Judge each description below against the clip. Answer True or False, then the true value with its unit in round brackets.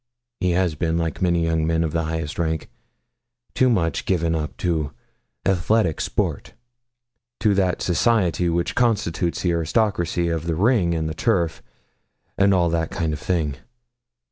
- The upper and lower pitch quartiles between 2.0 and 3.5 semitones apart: True (2.4 semitones)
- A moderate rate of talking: True (155 wpm)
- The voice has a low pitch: True (85 Hz)